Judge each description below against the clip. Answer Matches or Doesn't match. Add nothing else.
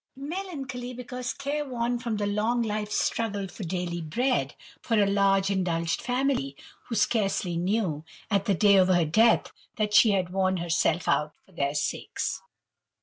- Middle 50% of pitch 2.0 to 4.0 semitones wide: Doesn't match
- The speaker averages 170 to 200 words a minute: Doesn't match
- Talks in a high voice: Matches